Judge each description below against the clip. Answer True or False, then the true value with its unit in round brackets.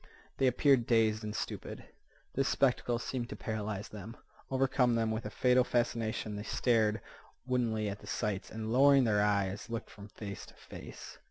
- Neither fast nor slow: True (170 wpm)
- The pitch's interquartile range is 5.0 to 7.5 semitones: False (2.9 semitones)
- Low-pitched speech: True (115 Hz)